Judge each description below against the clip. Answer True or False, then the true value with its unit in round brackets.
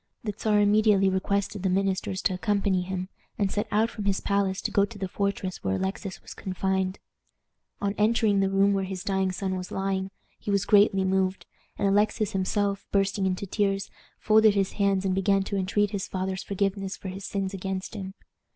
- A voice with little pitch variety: True (1.2 semitones)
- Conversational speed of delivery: True (190 wpm)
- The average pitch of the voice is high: True (195 Hz)